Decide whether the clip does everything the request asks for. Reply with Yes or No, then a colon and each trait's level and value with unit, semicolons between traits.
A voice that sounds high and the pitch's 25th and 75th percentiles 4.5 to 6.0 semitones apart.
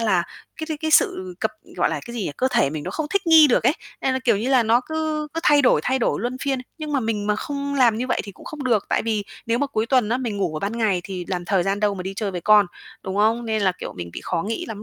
Yes: high, 225 Hz; average, 4.8 semitones